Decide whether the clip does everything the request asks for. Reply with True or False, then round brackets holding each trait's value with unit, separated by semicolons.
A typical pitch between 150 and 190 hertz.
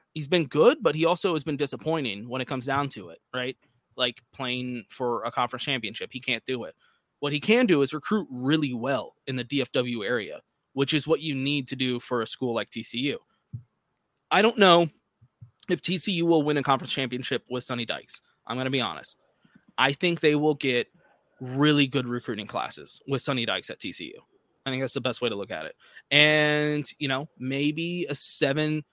False (135 Hz)